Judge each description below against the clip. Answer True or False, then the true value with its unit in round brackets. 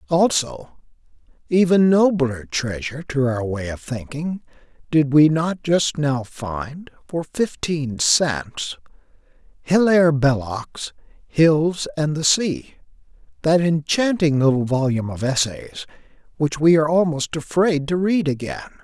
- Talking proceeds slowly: True (120 wpm)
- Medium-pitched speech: True (155 Hz)